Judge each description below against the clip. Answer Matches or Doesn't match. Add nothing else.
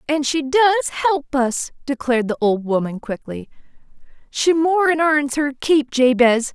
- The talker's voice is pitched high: Matches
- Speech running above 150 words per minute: Doesn't match